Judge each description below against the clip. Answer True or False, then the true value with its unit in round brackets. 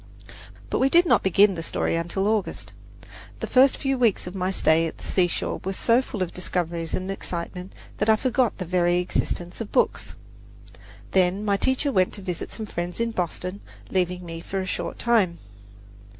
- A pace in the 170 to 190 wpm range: True (185 wpm)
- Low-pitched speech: False (185 Hz)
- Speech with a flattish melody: False (3.6 semitones)